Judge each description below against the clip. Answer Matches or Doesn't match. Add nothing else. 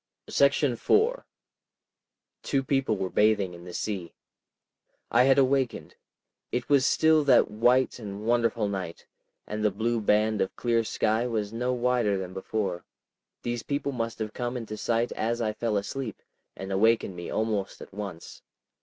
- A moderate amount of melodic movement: Matches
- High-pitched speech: Doesn't match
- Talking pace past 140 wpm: Matches